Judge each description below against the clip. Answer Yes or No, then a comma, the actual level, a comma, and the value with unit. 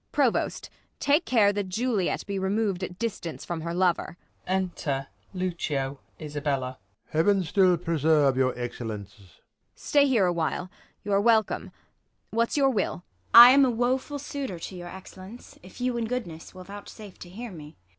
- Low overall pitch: No, medium, 185 Hz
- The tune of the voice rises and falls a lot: Yes, wide, 5.8 semitones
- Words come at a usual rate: Yes, average, 165 wpm